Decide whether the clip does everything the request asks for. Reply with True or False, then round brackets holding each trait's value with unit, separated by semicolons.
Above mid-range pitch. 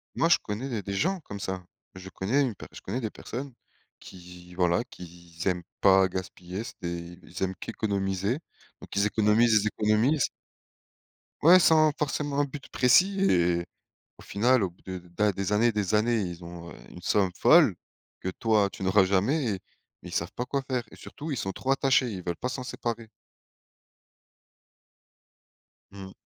False (105 Hz)